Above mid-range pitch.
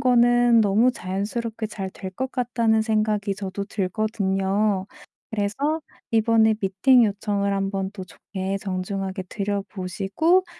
Yes: high, 205 Hz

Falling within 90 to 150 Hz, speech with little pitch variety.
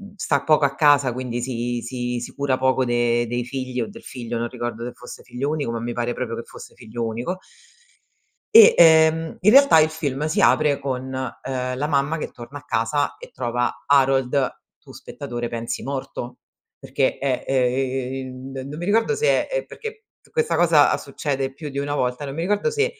No: low, 135 Hz; average, 3.6 semitones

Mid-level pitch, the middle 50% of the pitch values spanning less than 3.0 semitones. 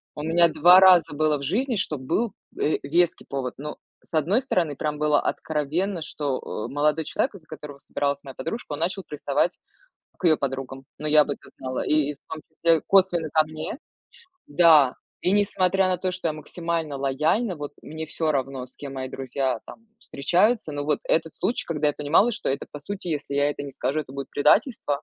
No: medium, 155 Hz; average, 3.6 semitones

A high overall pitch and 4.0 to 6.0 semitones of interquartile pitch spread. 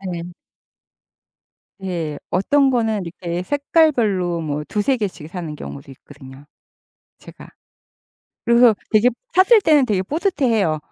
No: high, 195 Hz; wide, 7.4 semitones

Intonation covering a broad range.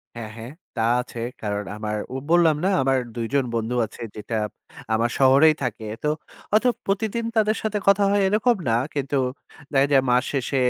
Yes: wide, 9.0 semitones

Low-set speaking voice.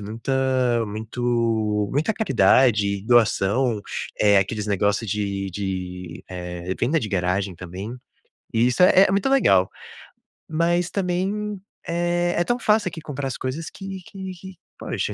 Yes: low, 120 Hz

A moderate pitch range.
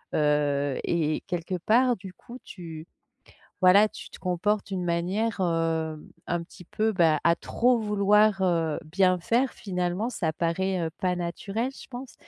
Yes: average, 4.0 semitones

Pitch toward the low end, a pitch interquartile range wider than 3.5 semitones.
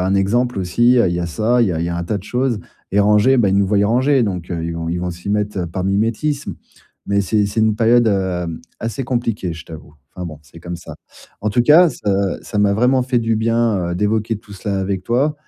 Yes: low, 105 Hz; average, 4.6 semitones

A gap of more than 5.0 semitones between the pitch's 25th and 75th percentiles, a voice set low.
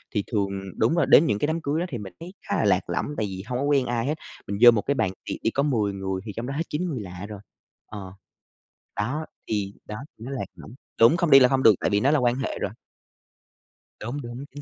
Yes: wide, 5.6 semitones; low, 120 Hz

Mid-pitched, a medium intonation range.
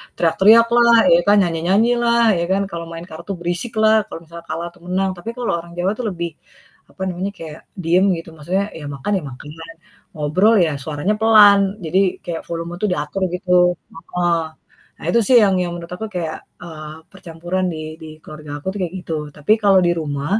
Yes: medium, 175 Hz; average, 3.4 semitones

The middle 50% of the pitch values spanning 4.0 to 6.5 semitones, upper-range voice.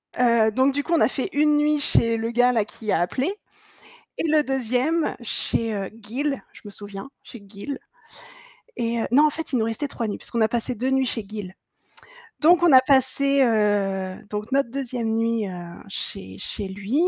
Yes: average, 4.6 semitones; high, 235 Hz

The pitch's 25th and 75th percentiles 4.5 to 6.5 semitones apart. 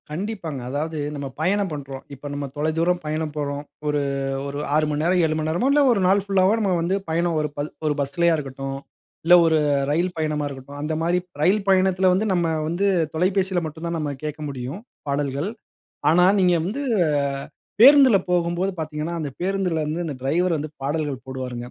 No: average, 3.9 semitones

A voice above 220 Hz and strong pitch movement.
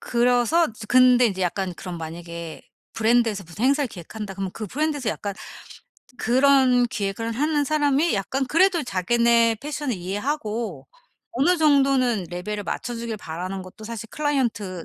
Yes: high, 235 Hz; wide, 5.8 semitones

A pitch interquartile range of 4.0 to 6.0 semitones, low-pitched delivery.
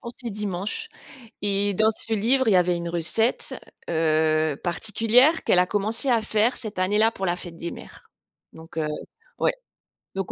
No: average, 4.4 semitones; high, 200 Hz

